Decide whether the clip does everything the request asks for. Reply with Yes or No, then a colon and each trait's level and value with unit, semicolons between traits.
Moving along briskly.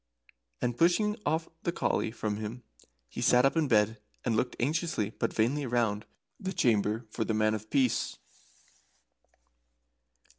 No: average, 140 wpm